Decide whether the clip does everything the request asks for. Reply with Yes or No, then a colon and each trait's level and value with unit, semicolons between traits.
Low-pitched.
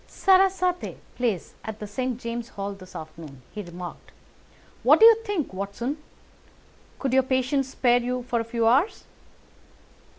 No: high, 245 Hz